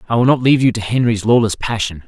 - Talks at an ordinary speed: No, fast, 260 wpm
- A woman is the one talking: No, male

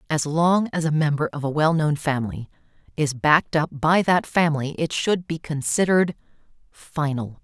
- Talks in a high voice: No, medium, 155 Hz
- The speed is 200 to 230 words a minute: No, average, 155 wpm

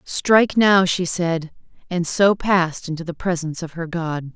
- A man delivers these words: No, female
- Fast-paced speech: No, average, 180 wpm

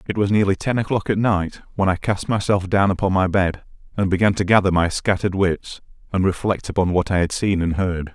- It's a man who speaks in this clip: Yes, male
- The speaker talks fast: Yes, fast, 230 wpm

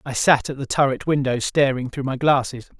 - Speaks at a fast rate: Yes, fast, 215 wpm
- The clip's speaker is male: Yes, male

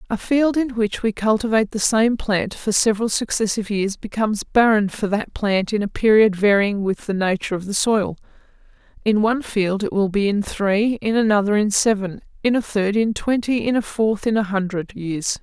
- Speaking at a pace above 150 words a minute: Yes, average, 200 wpm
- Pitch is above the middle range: Yes, high, 210 Hz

